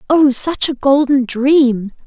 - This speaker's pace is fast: No, average, 145 wpm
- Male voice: No, female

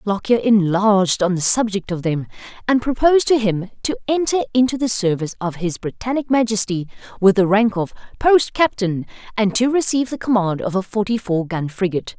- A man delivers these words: No, female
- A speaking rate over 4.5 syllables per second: Yes, 5.6 syllables/s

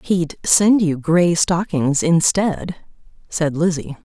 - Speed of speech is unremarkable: No, slow, 115 wpm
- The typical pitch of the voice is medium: Yes, medium, 170 Hz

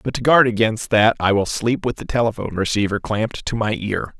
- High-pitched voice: No, low, 110 Hz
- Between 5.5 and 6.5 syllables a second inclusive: Yes, 5.8 syllables/s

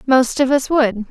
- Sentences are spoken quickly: Yes, fast, 215 wpm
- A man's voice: No, female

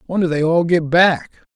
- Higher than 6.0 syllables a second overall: No, 5.0 syllables/s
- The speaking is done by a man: Yes, male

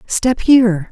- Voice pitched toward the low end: No, high, 220 Hz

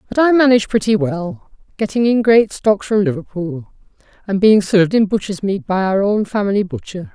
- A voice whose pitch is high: Yes, high, 205 Hz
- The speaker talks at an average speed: Yes, average, 185 wpm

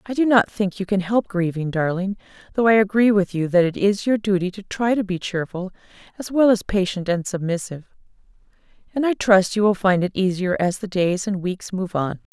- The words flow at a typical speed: No, fast, 220 wpm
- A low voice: No, high, 195 Hz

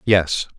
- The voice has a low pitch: Yes, very low, 90 Hz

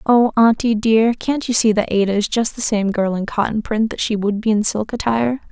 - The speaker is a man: No, female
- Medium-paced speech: No, fast, 250 wpm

